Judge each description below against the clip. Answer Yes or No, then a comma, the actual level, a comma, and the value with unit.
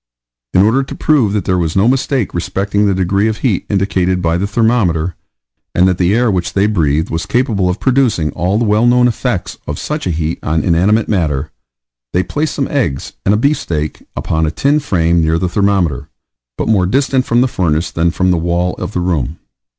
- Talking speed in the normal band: No, fast, 210 wpm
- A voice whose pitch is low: Yes, very low, 95 Hz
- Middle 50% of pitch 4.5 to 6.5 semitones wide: Yes, average, 5.0 semitones